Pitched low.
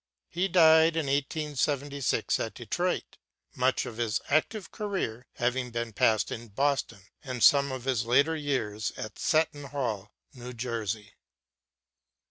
Yes: low, 130 Hz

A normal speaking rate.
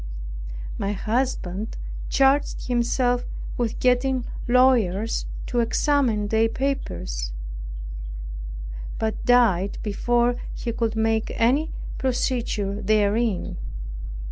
No: slow, 85 wpm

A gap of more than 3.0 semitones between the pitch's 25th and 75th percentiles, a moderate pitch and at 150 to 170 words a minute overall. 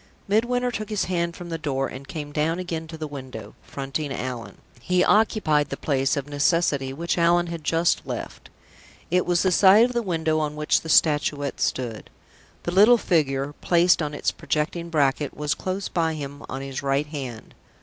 No: average, 3.8 semitones; medium, 155 Hz; average, 185 wpm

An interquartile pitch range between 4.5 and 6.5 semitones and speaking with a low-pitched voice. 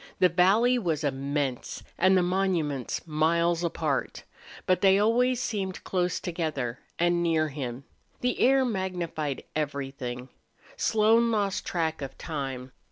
No: average, 5.1 semitones; medium, 170 Hz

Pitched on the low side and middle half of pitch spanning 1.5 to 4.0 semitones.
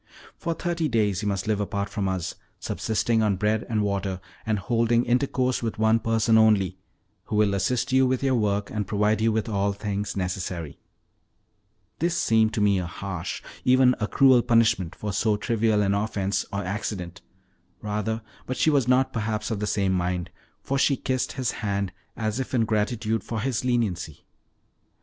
Yes: low, 110 Hz; average, 2.9 semitones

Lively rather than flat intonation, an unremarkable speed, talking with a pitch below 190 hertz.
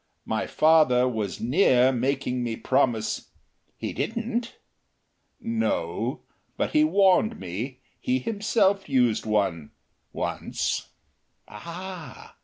No: wide, 8.3 semitones; slow, 100 wpm; low, 135 Hz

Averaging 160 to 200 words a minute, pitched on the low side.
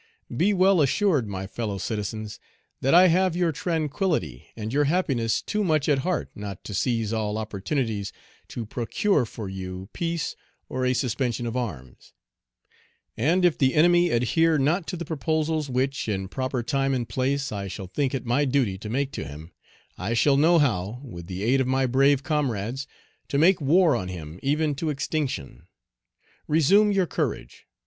Yes: average, 170 wpm; low, 130 Hz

